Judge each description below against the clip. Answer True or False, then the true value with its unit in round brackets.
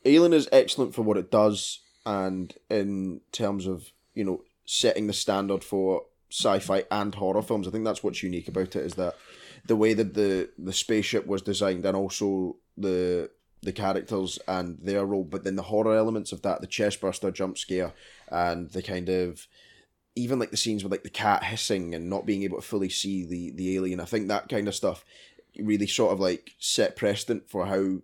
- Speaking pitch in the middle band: False (100 Hz)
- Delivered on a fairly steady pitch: True (2.2 semitones)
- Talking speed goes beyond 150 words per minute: True (200 wpm)